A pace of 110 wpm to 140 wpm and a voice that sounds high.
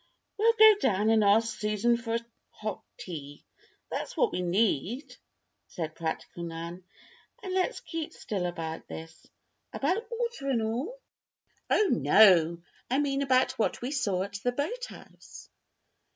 Yes: slow, 135 wpm; high, 225 Hz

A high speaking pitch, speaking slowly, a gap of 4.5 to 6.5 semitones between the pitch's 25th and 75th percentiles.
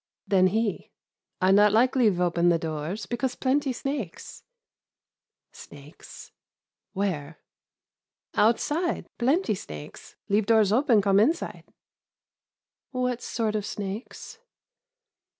Yes: high, 210 Hz; slow, 100 wpm; average, 5.1 semitones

